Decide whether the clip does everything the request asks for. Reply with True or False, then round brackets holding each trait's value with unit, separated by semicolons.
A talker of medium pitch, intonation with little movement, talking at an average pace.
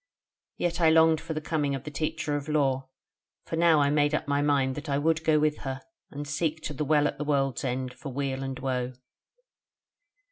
False (145 Hz; 2.3 semitones; 215 wpm)